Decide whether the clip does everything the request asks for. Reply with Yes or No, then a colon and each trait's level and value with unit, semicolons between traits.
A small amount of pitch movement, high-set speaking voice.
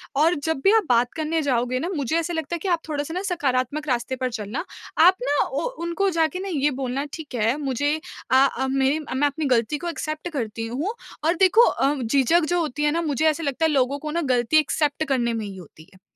No: average, 4.2 semitones; very high, 290 Hz